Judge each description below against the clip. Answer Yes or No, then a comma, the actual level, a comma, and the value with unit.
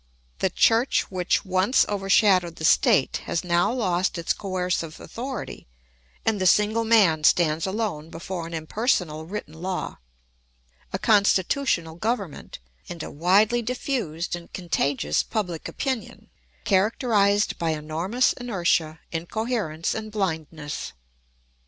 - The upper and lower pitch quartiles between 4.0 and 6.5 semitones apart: Yes, average, 4.8 semitones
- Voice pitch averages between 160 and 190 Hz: Yes, medium, 185 Hz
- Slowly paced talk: Yes, slow, 115 wpm